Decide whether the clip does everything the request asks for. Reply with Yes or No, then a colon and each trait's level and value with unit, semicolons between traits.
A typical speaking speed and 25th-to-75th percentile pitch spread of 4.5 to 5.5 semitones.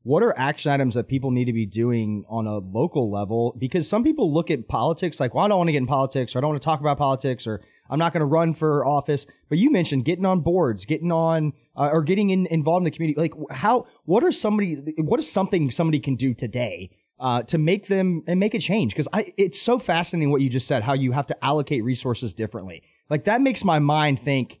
No: fast, 250 wpm; average, 4.9 semitones